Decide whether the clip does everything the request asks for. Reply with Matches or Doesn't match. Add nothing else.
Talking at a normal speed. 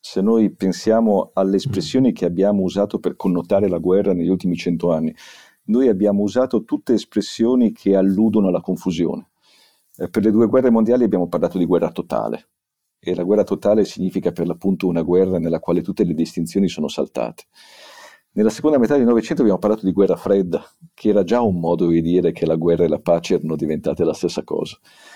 Doesn't match